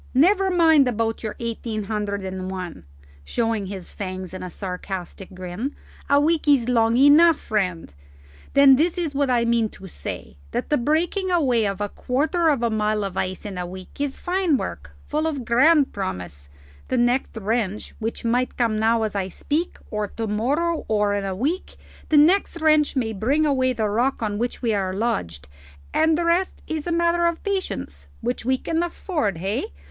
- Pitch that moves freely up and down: Yes, wide, 7.1 semitones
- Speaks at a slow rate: No, average, 190 wpm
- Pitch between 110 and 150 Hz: No, high, 235 Hz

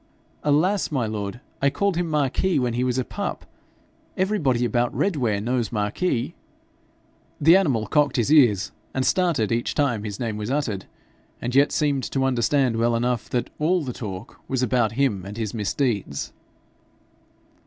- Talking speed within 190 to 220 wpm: No, average, 160 wpm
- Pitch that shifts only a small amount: No, average, 4.6 semitones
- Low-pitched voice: Yes, low, 125 Hz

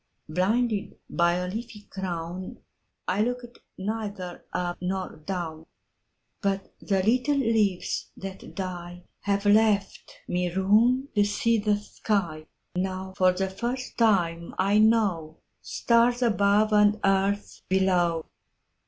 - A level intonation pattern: No, average, 3.2 semitones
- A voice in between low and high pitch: No, high, 195 Hz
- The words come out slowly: Yes, slow, 100 wpm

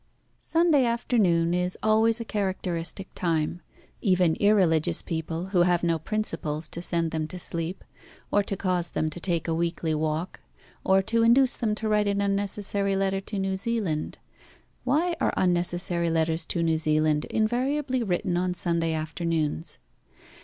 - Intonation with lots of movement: No, average, 4.0 semitones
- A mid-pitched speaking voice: Yes, medium, 180 Hz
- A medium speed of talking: Yes, average, 155 wpm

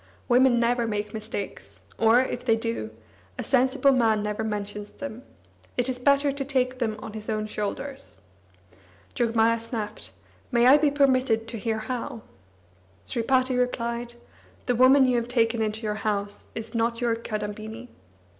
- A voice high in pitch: Yes, high, 230 Hz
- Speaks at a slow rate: No, average, 155 wpm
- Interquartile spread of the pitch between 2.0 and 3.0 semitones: Yes, narrow, 2.6 semitones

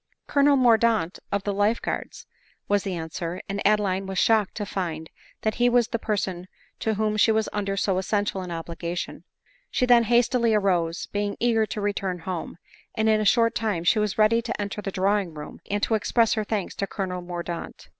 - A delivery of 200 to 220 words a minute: Yes, fast, 205 wpm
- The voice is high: Yes, high, 205 Hz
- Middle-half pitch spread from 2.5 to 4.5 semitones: Yes, average, 3.0 semitones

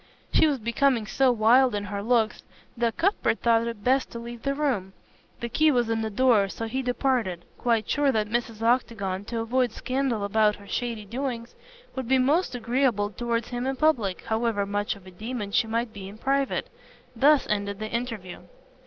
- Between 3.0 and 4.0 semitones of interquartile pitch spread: Yes, average, 3.5 semitones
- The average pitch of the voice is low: No, high, 235 Hz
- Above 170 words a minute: Yes, average, 190 wpm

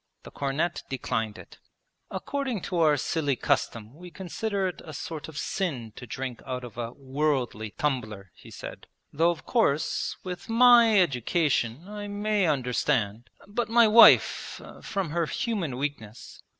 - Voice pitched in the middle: Yes, medium, 150 Hz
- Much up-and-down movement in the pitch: Yes, wide, 7.8 semitones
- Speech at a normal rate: Yes, average, 150 wpm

